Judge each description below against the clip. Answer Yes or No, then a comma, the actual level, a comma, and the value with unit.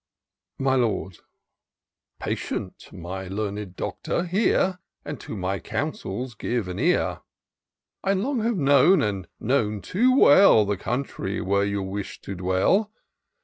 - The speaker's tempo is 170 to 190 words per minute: No, slow, 135 wpm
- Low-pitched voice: Yes, low, 110 Hz